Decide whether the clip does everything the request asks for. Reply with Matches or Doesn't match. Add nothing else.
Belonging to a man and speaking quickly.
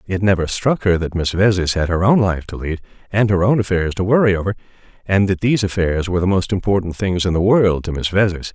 Matches